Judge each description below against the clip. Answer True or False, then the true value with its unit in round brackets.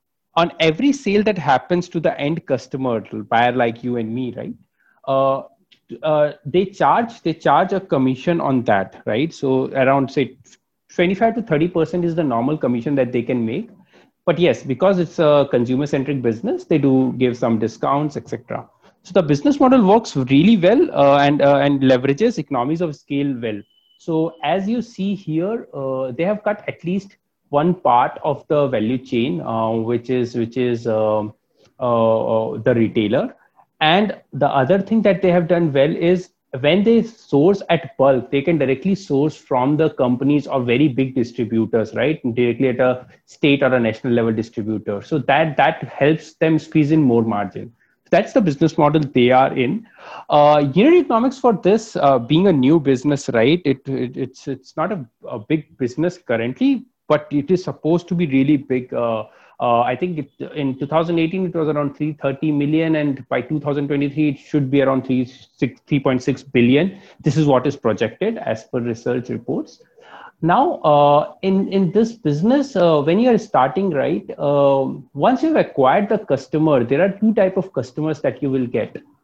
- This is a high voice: False (145 Hz)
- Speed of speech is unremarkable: True (180 wpm)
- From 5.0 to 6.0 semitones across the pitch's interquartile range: True (5.3 semitones)